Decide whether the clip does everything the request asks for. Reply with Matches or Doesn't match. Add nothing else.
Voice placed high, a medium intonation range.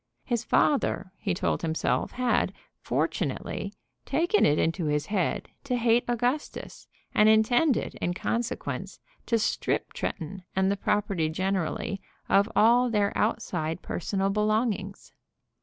Matches